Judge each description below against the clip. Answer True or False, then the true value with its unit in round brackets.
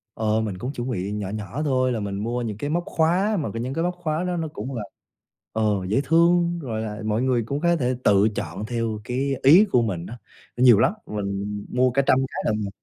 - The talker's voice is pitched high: False (120 Hz)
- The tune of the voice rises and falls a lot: True (5.8 semitones)